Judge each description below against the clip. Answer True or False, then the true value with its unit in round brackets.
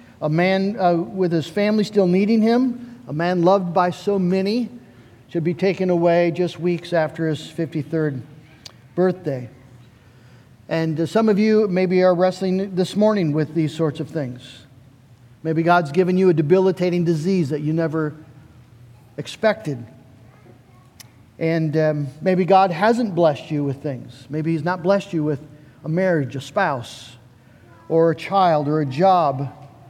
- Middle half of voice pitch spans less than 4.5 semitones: False (5.3 semitones)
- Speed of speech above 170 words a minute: False (155 wpm)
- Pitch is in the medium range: True (160 Hz)